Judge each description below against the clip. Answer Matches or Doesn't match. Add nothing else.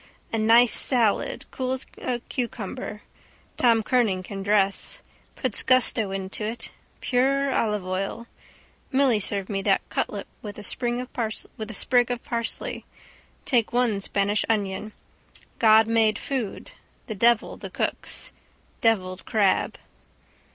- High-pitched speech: Matches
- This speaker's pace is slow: Matches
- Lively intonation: Doesn't match